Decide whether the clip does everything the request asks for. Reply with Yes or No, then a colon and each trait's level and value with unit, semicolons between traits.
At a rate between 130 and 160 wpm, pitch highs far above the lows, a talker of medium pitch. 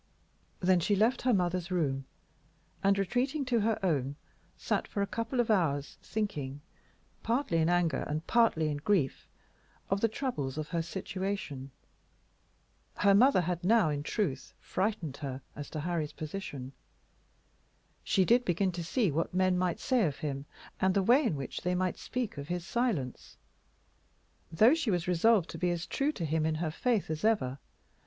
No: average, 170 wpm; wide, 5.7 semitones; medium, 180 Hz